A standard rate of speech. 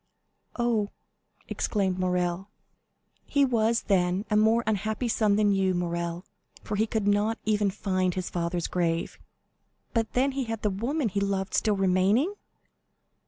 Yes: average, 150 wpm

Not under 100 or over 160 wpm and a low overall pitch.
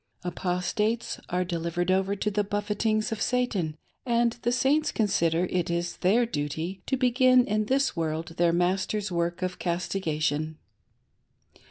No: average, 140 wpm; high, 190 Hz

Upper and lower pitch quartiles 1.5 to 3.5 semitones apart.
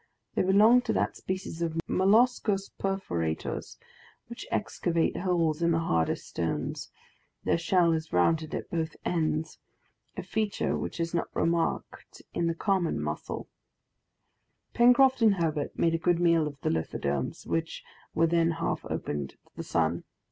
Yes: average, 3.1 semitones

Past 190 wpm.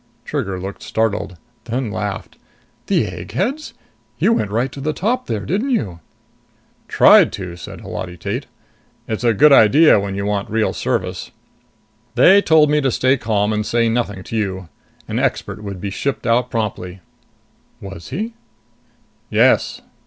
No: average, 155 wpm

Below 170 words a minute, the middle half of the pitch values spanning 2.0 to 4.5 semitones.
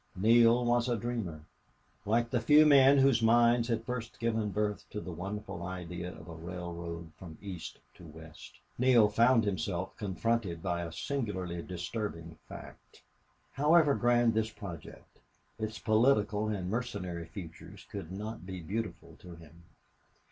No: average, 145 wpm; average, 5.2 semitones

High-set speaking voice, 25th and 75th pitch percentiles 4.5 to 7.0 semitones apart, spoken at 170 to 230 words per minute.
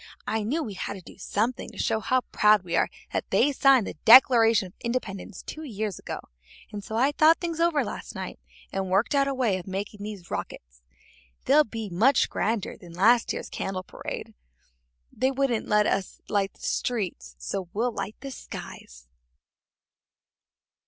Yes: high, 215 Hz; average, 4.9 semitones; average, 175 wpm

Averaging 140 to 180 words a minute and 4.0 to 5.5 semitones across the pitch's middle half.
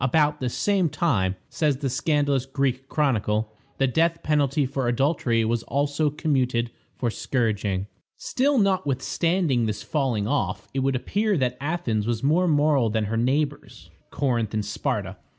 Yes: average, 150 wpm; average, 4.5 semitones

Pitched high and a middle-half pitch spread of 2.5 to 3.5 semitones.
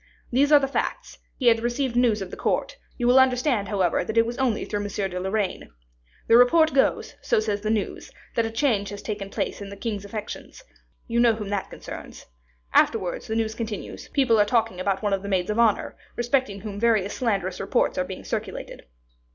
Yes: high, 220 Hz; average, 3.1 semitones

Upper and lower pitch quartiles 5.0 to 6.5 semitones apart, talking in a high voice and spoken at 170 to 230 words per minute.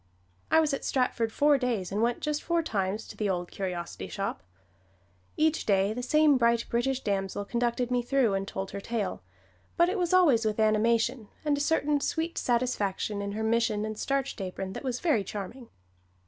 Yes: average, 5.3 semitones; high, 235 Hz; average, 190 wpm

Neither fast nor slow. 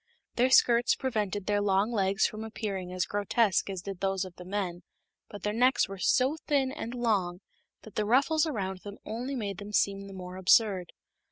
Yes: average, 190 wpm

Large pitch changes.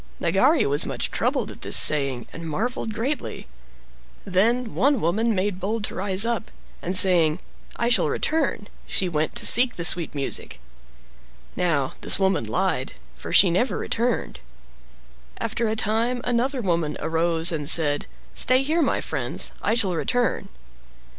Yes: wide, 6.0 semitones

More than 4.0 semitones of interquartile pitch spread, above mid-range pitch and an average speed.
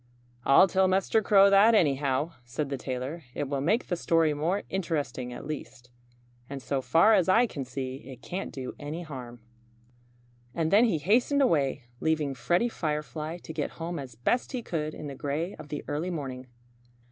No: average, 5.2 semitones; medium, 155 Hz; average, 180 wpm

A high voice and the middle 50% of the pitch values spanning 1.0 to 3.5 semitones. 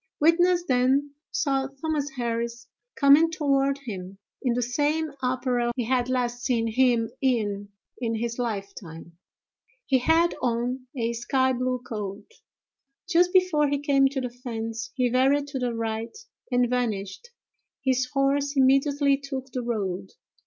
Yes: very high, 255 Hz; average, 3.1 semitones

